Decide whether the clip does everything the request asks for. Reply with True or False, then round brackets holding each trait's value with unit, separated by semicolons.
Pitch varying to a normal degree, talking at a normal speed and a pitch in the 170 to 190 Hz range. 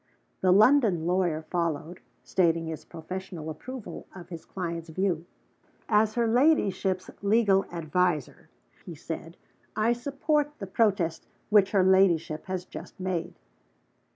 False (3.9 semitones; 125 wpm; 185 Hz)